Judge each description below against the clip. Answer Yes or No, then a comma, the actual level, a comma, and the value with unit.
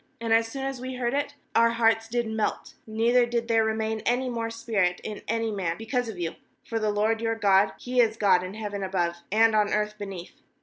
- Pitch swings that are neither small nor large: No, narrow, 1.9 semitones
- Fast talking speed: Yes, fast, 225 wpm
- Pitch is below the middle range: No, high, 225 Hz